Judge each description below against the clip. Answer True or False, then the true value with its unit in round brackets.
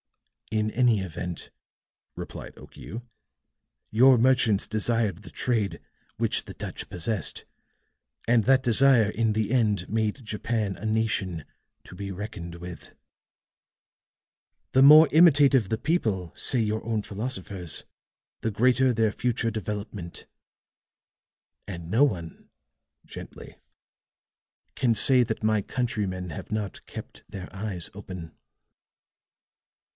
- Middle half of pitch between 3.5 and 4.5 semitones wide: True (3.8 semitones)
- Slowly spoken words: True (115 wpm)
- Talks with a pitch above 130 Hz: False (110 Hz)